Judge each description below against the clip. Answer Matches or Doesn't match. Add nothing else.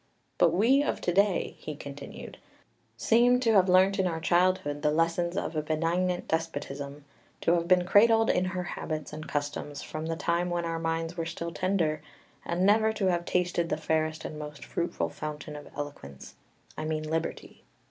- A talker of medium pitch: Matches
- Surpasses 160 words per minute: Matches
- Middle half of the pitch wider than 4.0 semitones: Doesn't match